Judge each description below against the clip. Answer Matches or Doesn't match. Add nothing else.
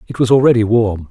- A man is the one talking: Matches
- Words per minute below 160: Doesn't match